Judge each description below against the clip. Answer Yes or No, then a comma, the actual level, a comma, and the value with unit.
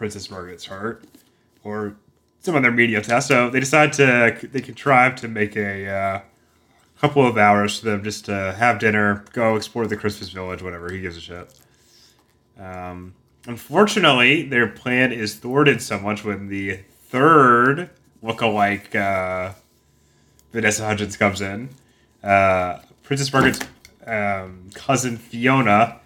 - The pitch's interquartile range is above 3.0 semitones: Yes, average, 3.8 semitones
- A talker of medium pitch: No, low, 105 Hz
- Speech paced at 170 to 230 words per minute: No, average, 140 wpm